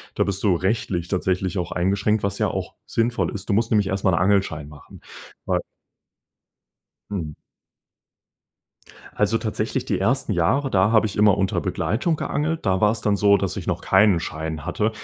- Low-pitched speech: Yes, low, 100 Hz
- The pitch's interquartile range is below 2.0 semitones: No, average, 2.9 semitones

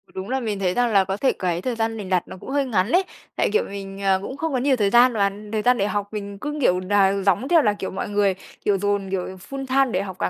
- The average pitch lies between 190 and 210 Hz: Yes, high, 205 Hz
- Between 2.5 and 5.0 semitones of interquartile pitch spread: Yes, average, 4.3 semitones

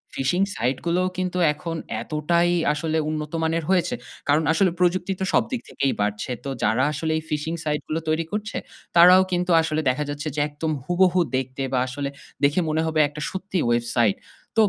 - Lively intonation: No, average, 3.8 semitones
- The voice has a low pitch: No, medium, 160 Hz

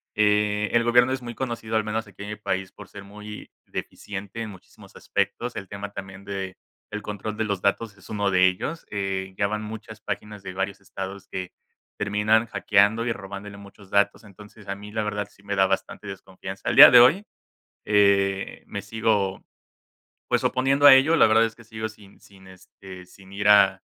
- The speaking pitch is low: Yes, low, 105 Hz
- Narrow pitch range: Yes, narrow, 2.0 semitones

